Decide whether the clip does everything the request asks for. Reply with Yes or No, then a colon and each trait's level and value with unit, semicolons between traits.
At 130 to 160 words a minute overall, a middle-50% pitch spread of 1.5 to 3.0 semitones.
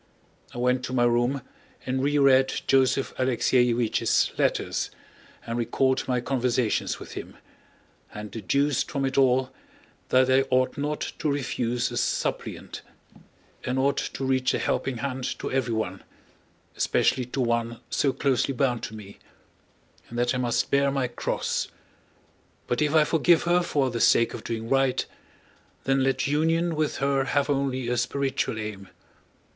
Yes: average, 145 wpm; narrow, 2.4 semitones